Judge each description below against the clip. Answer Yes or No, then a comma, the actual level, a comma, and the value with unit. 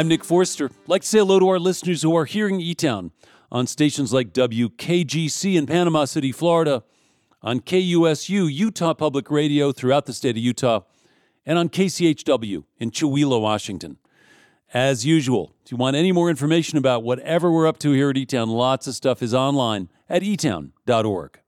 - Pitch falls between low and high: Yes, medium, 150 Hz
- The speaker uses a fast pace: No, average, 180 wpm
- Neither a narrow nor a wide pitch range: Yes, average, 4.9 semitones